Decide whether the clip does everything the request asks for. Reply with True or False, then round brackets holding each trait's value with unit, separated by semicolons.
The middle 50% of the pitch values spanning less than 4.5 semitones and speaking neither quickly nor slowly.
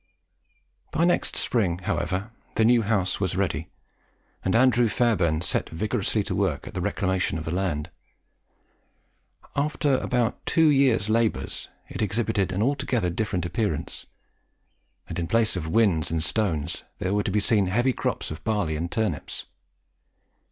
False (4.9 semitones; 150 wpm)